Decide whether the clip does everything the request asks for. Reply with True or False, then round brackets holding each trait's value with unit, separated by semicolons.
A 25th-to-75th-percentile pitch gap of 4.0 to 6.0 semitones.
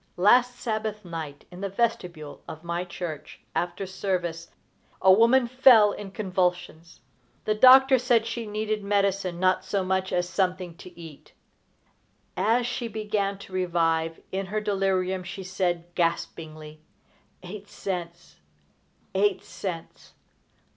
False (3.4 semitones)